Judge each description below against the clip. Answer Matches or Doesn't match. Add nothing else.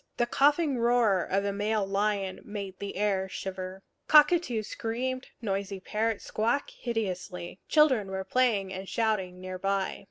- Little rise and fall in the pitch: Doesn't match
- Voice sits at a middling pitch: Doesn't match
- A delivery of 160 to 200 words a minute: Doesn't match